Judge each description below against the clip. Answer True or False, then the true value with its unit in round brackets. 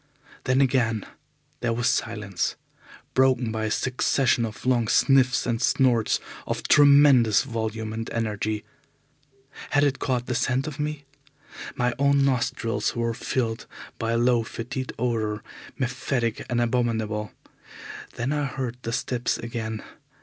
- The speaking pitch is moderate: False (120 Hz)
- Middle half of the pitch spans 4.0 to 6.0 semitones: False (2.6 semitones)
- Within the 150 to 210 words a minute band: False (135 wpm)